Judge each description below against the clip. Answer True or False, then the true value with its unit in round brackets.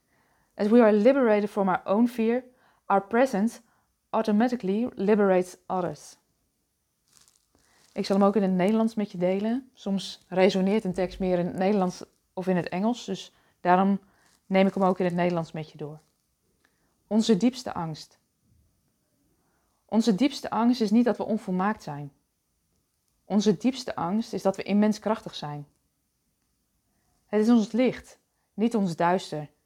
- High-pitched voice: True (195 Hz)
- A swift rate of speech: False (150 wpm)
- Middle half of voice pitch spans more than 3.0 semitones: True (3.7 semitones)